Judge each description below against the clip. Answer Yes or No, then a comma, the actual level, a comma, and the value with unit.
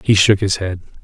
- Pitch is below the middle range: Yes, low, 100 Hz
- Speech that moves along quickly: Yes, fast, 230 wpm